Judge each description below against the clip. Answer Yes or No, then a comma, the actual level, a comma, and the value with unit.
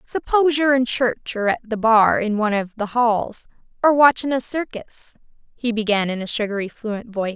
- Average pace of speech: Yes, average, 190 wpm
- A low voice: No, high, 230 Hz